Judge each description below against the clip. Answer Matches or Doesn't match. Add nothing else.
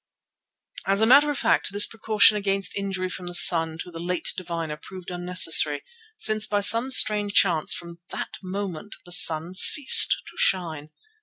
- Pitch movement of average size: Matches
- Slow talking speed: Doesn't match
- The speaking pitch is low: Doesn't match